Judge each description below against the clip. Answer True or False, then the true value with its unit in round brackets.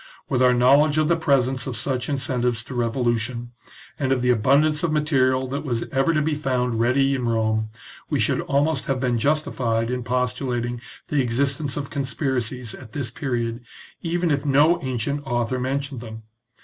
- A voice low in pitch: True (130 Hz)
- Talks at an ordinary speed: True (175 wpm)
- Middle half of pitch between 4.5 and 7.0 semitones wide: False (2.8 semitones)